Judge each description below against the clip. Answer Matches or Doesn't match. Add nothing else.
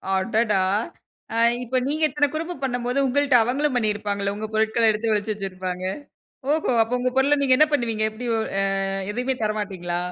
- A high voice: Matches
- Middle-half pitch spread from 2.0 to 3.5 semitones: Doesn't match